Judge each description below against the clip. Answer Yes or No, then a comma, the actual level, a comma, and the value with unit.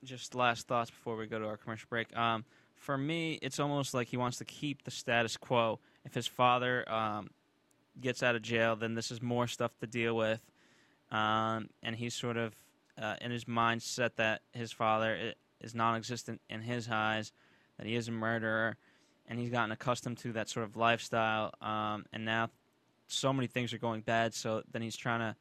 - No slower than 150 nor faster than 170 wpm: No, average, 200 wpm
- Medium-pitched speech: No, low, 115 Hz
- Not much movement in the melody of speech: Yes, narrow, 1.7 semitones